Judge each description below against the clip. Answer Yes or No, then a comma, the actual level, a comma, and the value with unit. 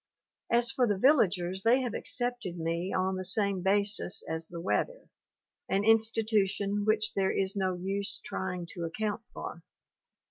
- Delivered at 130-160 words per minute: Yes, average, 150 wpm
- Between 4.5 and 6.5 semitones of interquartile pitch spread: No, average, 2.9 semitones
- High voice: Yes, high, 200 Hz